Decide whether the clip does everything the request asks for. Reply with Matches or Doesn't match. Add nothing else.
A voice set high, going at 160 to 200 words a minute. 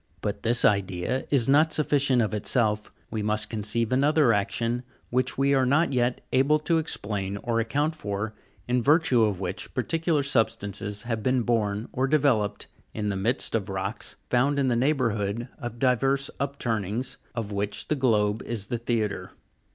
Doesn't match